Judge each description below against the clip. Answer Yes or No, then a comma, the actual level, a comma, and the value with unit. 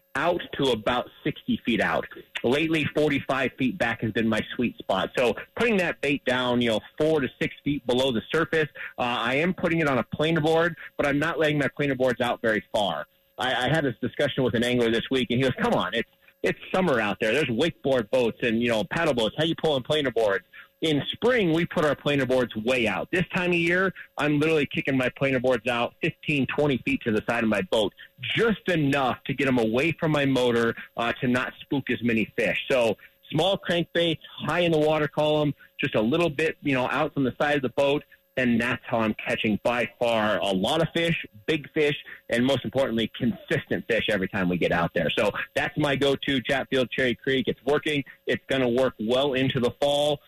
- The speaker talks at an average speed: No, fast, 225 wpm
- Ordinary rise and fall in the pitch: Yes, average, 3.9 semitones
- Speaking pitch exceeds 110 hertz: Yes, medium, 140 Hz